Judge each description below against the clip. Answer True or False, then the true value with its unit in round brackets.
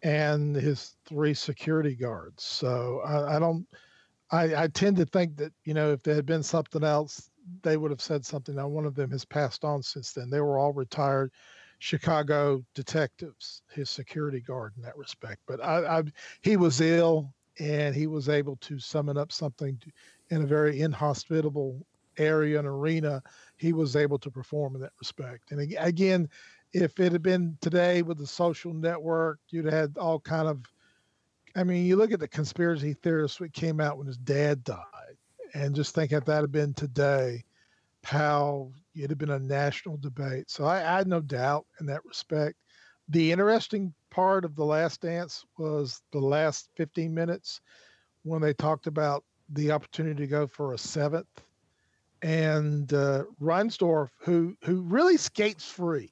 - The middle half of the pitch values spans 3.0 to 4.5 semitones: False (2.5 semitones)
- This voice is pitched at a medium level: True (150 Hz)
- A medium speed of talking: True (175 wpm)